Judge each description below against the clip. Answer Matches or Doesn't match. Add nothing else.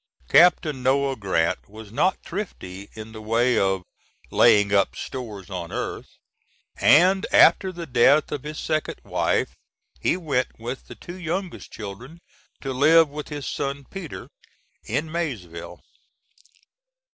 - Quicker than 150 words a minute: Doesn't match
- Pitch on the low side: Matches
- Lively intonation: Matches